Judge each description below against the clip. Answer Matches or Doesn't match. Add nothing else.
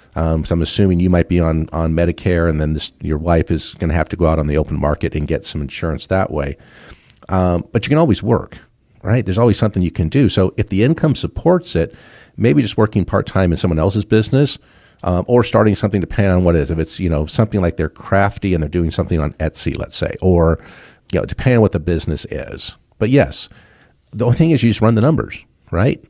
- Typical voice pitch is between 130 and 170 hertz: Doesn't match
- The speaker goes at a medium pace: Doesn't match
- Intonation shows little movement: Doesn't match